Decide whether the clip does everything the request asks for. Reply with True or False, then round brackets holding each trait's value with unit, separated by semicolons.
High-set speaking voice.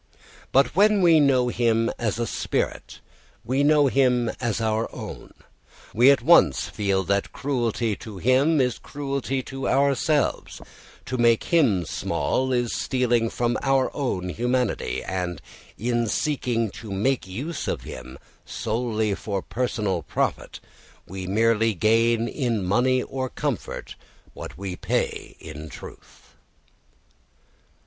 False (120 Hz)